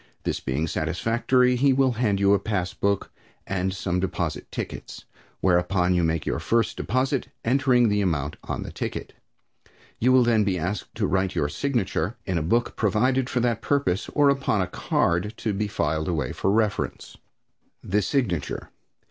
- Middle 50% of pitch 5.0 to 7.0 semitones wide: Yes, wide, 5.5 semitones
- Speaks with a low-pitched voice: Yes, low, 100 Hz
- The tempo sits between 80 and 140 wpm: No, average, 165 wpm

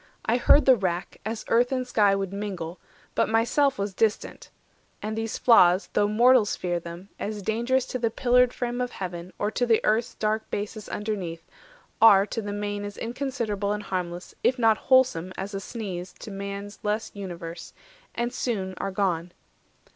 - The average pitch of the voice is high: Yes, high, 210 Hz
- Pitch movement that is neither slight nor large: Yes, average, 3.5 semitones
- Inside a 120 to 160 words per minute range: No, average, 175 wpm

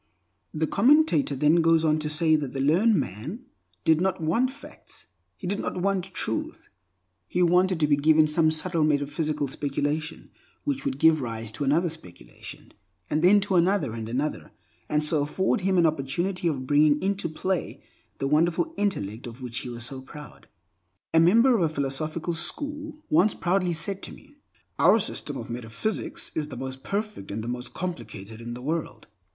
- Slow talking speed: No, average, 180 wpm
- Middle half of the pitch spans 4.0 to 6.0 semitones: Yes, average, 5.1 semitones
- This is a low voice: No, medium, 155 Hz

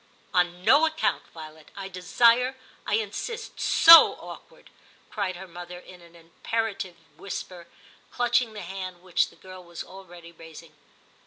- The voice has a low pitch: No, medium, 185 Hz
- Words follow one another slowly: No, average, 155 wpm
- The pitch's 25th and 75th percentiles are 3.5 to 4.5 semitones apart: Yes, average, 3.9 semitones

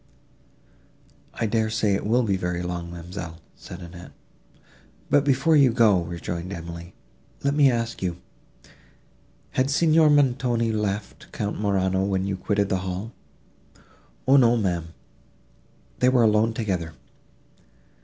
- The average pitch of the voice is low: Yes, low, 100 Hz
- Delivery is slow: Yes, slow, 125 wpm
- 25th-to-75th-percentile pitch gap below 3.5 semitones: No, average, 5.2 semitones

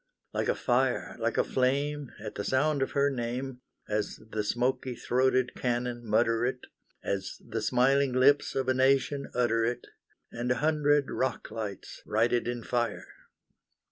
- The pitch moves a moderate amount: No, narrow, 2.2 semitones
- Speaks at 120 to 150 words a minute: No, average, 160 wpm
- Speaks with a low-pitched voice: Yes, low, 125 Hz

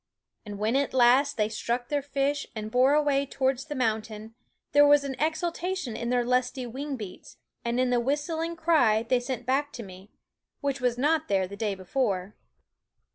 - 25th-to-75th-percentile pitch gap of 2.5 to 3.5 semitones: No, average, 4.4 semitones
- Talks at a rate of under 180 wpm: No, average, 185 wpm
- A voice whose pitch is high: Yes, very high, 255 Hz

